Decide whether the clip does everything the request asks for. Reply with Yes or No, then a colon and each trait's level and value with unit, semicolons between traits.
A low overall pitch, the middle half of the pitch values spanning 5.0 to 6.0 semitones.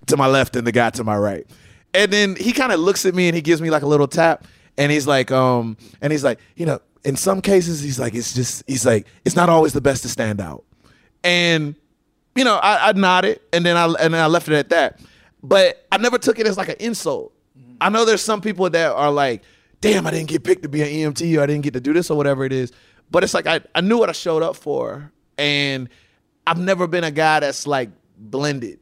No: medium, 155 Hz; wide, 5.4 semitones